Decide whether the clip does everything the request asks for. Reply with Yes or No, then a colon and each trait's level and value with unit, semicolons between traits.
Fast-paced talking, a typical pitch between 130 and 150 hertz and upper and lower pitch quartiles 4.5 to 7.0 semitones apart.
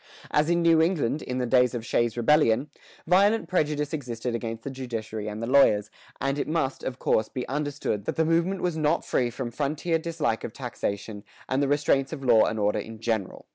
Yes: fast, 210 wpm; low, 135 Hz; average, 5.0 semitones